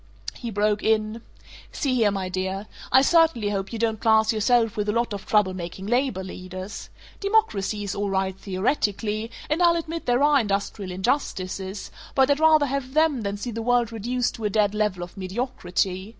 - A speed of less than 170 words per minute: No, average, 185 wpm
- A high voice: Yes, high, 215 Hz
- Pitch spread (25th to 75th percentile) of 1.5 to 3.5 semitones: No, average, 4.3 semitones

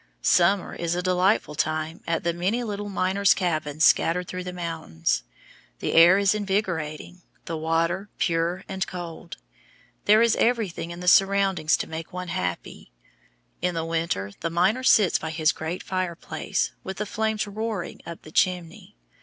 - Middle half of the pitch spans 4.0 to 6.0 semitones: No, average, 3.0 semitones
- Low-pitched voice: No, medium, 180 Hz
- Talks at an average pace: Yes, average, 160 wpm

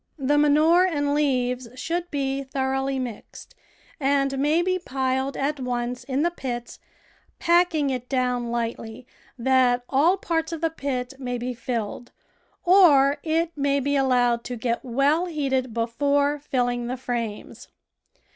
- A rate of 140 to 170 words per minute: Yes, average, 145 wpm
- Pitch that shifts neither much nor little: Yes, average, 3.0 semitones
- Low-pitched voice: No, very high, 270 Hz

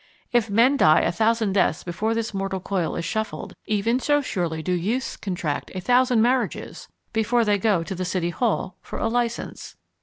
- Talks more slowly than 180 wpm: No, average, 185 wpm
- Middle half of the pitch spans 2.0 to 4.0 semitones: No, average, 4.4 semitones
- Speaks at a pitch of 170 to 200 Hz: No, high, 210 Hz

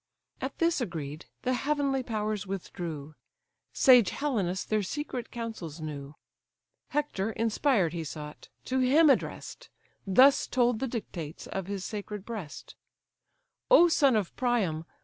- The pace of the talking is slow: Yes, slow, 130 wpm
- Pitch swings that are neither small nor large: No, wide, 7.0 semitones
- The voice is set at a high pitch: Yes, high, 215 Hz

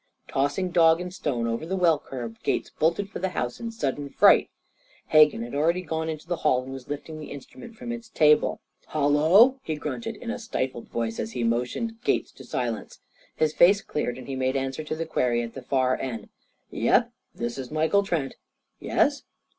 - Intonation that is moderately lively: No, wide, 5.7 semitones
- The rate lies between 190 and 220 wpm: Yes, average, 195 wpm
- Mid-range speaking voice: Yes, medium, 150 Hz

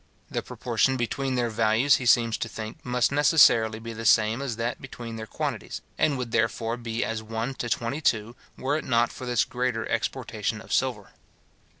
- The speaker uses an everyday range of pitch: No, narrow, 2.1 semitones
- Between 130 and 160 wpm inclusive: No, average, 190 wpm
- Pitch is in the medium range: No, low, 115 Hz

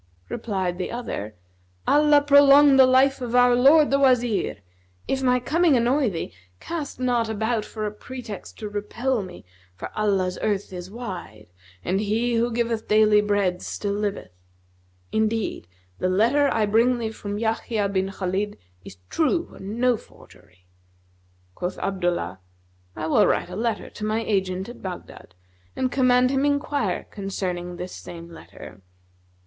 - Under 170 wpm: Yes, average, 150 wpm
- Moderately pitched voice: No, high, 220 Hz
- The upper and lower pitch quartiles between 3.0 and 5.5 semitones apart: Yes, average, 4.7 semitones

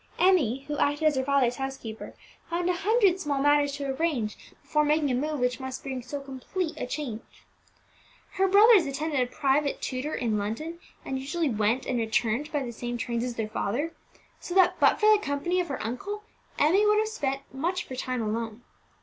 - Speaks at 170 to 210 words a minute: Yes, average, 200 wpm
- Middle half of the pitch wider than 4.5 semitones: Yes, average, 4.9 semitones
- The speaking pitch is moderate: No, very high, 280 Hz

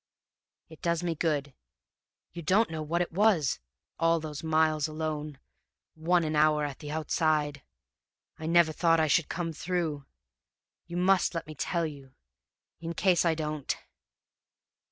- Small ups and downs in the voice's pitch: Yes, narrow, 1.9 semitones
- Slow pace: No, average, 150 wpm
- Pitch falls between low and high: Yes, medium, 160 Hz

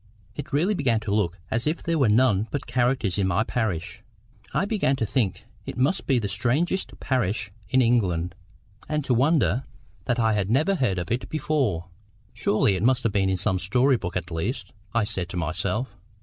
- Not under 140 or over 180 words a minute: No, average, 190 wpm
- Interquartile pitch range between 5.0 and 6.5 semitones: Yes, wide, 5.6 semitones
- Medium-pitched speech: No, low, 115 Hz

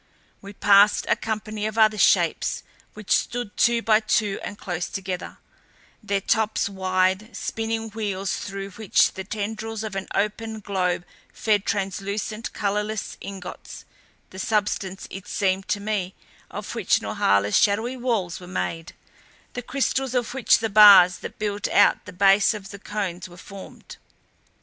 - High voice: Yes, high, 205 Hz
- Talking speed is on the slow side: No, average, 150 wpm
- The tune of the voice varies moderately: No, narrow, 2.3 semitones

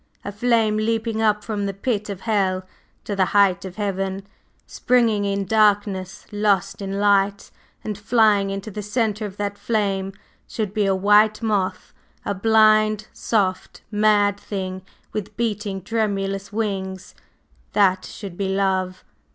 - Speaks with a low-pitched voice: No, high, 205 Hz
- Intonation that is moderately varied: No, narrow, 1.8 semitones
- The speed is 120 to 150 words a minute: Yes, average, 145 wpm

